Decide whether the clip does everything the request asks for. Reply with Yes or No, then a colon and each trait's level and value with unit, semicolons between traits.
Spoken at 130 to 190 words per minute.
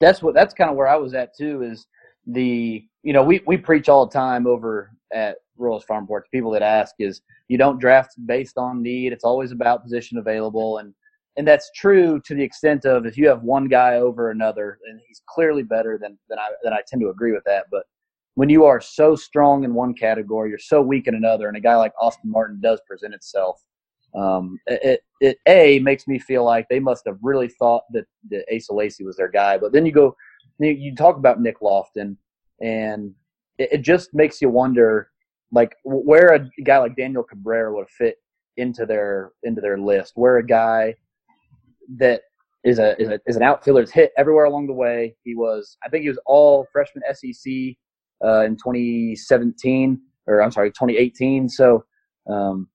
No: average, 200 wpm